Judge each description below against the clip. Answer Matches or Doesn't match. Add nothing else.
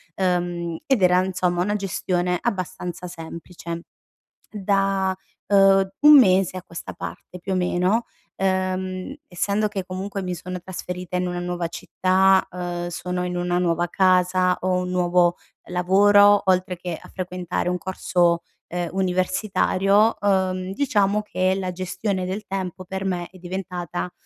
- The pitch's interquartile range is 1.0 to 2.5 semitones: Matches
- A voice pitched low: Doesn't match